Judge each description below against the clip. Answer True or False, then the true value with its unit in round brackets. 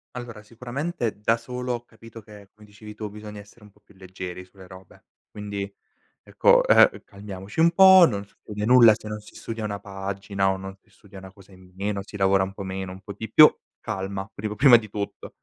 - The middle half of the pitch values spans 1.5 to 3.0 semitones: True (2.6 semitones)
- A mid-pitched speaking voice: False (105 Hz)